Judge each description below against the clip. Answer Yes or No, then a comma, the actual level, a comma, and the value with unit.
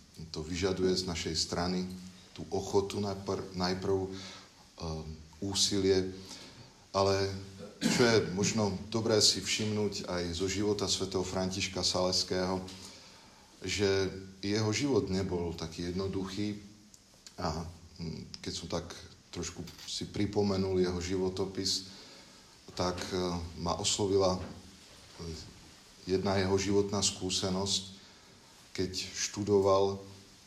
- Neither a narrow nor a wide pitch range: No, narrow, 1.4 semitones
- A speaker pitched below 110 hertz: Yes, very low, 95 Hz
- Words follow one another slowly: Yes, slow, 95 wpm